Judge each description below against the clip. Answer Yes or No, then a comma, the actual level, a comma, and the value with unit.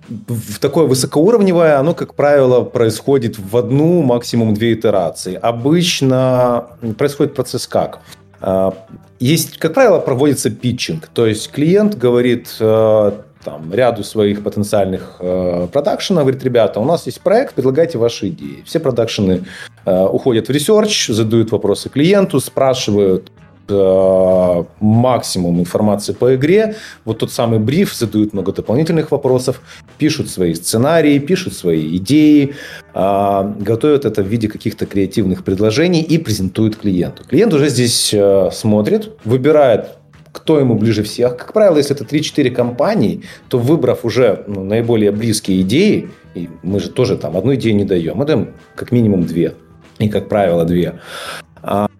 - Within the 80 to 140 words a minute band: Yes, average, 135 wpm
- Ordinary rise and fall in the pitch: No, wide, 5.8 semitones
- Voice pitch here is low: Yes, low, 115 Hz